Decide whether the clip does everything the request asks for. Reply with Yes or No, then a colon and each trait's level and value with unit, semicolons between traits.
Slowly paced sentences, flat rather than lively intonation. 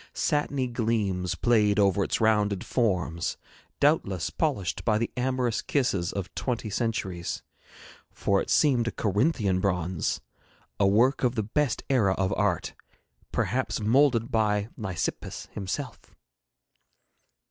No: slow, 120 wpm; average, 4.3 semitones